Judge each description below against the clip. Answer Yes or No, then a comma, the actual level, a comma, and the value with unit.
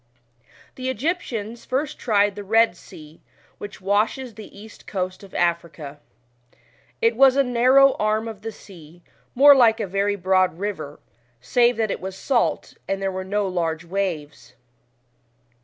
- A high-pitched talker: Yes, high, 205 Hz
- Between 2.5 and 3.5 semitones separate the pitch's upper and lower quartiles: No, average, 4.2 semitones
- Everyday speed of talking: Yes, average, 150 wpm